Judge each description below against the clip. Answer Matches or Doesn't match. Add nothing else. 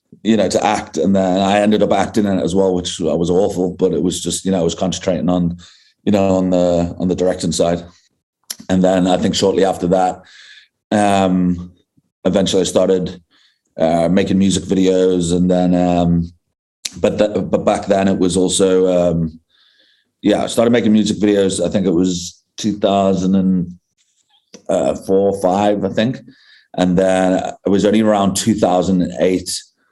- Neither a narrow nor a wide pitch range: Doesn't match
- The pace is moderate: Matches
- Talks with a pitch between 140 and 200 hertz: Doesn't match